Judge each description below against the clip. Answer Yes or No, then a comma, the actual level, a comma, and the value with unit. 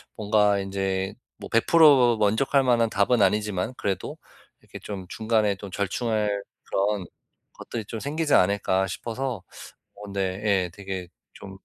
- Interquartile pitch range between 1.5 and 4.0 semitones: Yes, average, 3.0 semitones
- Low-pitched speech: Yes, low, 105 Hz